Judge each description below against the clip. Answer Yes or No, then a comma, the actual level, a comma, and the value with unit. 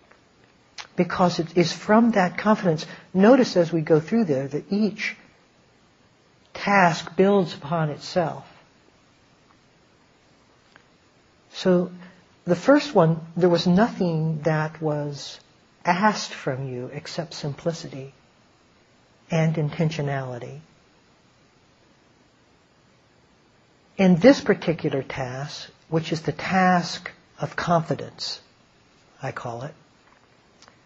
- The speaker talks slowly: Yes, slow, 90 wpm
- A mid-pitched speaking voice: Yes, medium, 170 Hz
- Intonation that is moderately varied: Yes, average, 3.6 semitones